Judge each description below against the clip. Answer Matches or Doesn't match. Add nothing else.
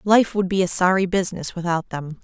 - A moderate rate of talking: Doesn't match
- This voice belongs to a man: Doesn't match